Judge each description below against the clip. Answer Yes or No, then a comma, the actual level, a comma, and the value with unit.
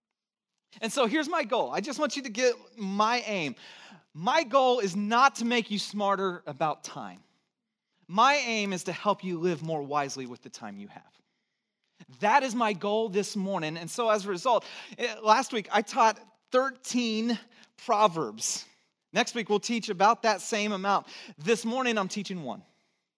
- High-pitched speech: Yes, high, 215 Hz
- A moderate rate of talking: Yes, average, 175 wpm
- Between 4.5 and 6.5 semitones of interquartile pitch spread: No, average, 3.7 semitones